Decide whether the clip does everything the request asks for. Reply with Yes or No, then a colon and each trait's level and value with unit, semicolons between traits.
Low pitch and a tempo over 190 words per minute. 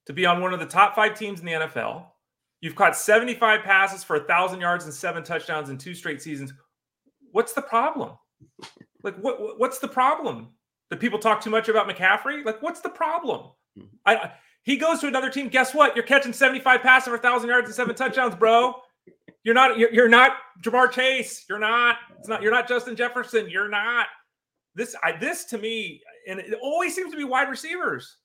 No: high, 235 Hz; fast, 205 wpm